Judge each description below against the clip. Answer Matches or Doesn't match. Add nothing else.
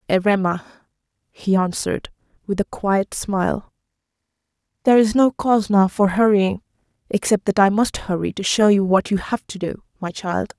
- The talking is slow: Doesn't match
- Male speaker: Doesn't match